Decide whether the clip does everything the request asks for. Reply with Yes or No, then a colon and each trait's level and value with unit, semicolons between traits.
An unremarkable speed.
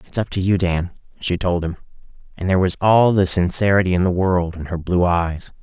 No: fast, 225 wpm